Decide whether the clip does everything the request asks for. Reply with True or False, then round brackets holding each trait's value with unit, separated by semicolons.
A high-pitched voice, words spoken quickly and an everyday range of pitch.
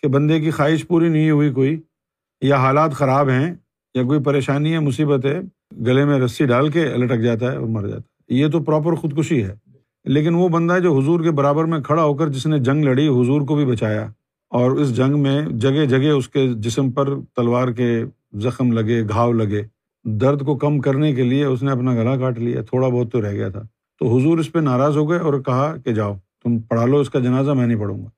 False (140 Hz; 235 wpm; 3.5 semitones)